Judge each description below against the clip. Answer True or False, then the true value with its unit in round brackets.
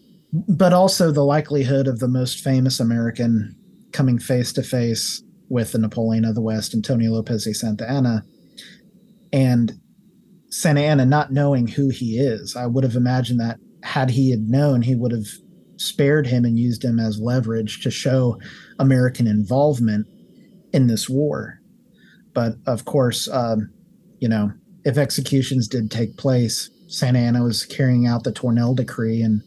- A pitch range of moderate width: True (3.6 semitones)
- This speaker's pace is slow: False (160 wpm)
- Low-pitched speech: True (125 Hz)